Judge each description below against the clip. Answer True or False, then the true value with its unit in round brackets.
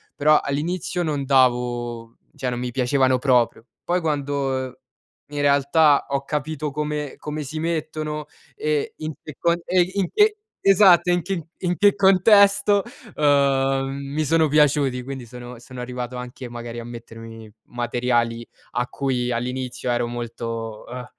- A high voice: False (140 Hz)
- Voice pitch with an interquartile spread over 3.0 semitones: True (4.1 semitones)